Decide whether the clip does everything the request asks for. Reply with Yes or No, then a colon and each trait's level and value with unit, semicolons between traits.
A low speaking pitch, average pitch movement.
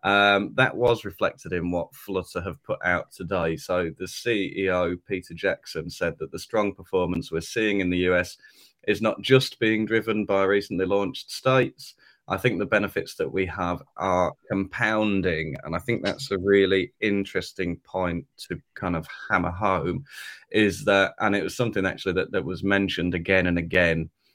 No: very low, 95 Hz; narrow, 2.3 semitones